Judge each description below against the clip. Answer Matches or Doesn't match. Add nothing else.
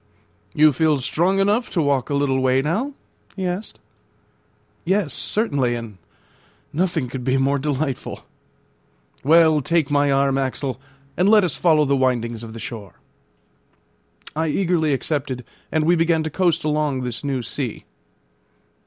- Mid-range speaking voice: Matches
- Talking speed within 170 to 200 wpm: Doesn't match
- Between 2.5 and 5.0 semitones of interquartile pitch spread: Matches